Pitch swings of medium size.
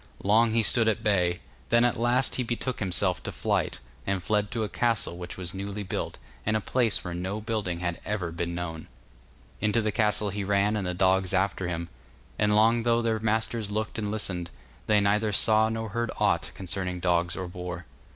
Yes: average, 3.5 semitones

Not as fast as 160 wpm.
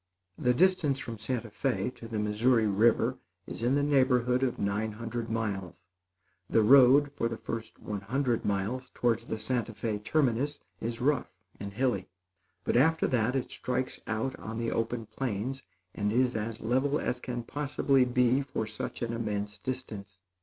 No: average, 165 wpm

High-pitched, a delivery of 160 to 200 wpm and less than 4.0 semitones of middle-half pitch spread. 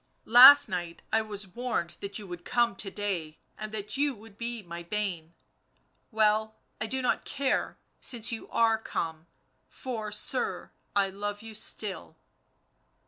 No: high, 210 Hz; average, 150 wpm; average, 2.9 semitones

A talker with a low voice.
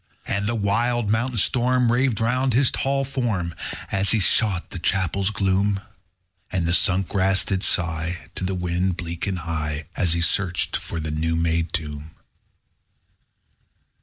Yes: very low, 95 Hz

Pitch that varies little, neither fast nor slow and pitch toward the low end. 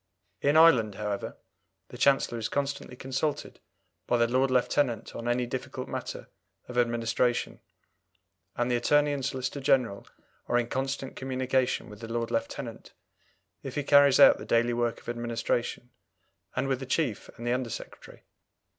Yes: narrow, 2.2 semitones; average, 155 wpm; low, 125 Hz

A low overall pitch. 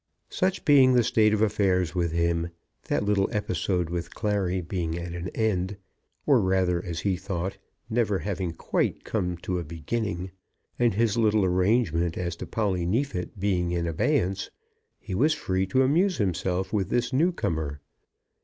Yes: very low, 95 Hz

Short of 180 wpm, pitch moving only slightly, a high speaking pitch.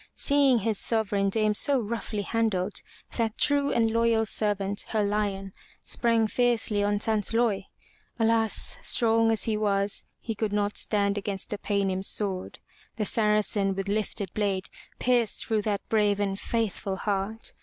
Yes: average, 145 wpm; narrow, 2.0 semitones; high, 210 Hz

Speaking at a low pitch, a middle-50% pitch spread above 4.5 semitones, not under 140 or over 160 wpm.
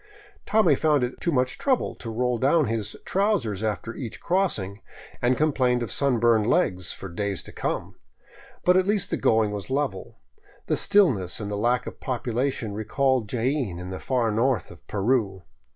No: low, 120 Hz; average, 4.9 semitones; average, 170 wpm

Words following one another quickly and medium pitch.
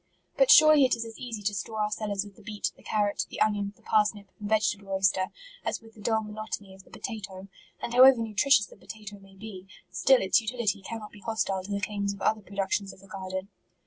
No: fast, 225 wpm; high, 210 Hz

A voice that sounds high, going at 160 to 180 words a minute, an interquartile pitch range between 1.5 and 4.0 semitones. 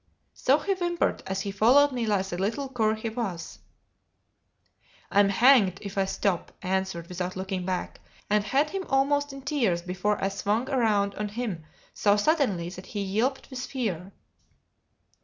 No: high, 210 Hz; average, 165 wpm; wide, 5.6 semitones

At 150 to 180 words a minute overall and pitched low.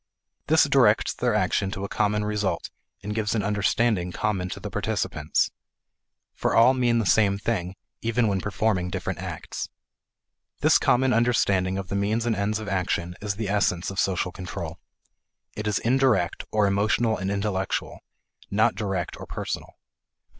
Yes: average, 160 wpm; low, 100 Hz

